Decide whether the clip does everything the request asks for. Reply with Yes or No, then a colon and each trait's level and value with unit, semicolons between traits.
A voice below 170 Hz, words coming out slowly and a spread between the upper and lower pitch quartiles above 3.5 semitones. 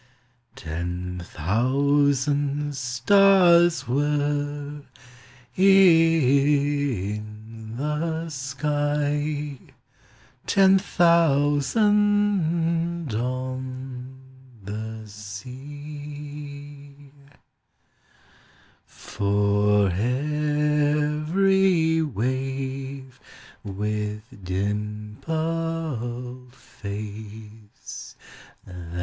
Yes: medium, 140 Hz; slow, 35 wpm; average, 5.3 semitones